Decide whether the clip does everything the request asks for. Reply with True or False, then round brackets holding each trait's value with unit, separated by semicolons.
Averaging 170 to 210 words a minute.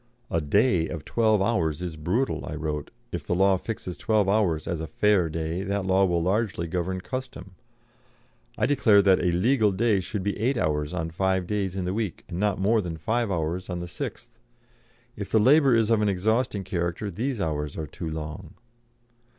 True (195 wpm)